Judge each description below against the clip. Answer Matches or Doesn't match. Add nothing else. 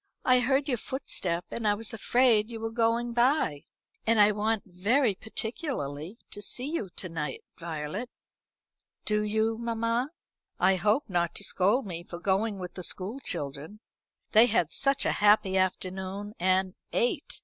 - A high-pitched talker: Matches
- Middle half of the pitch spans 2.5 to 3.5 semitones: Doesn't match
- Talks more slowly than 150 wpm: Doesn't match